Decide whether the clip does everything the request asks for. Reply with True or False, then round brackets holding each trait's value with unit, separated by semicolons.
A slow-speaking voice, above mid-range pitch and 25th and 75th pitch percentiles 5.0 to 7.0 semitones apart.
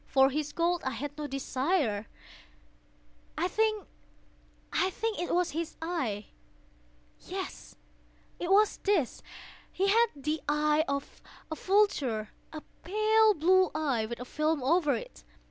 True (125 wpm; 315 Hz; 5.4 semitones)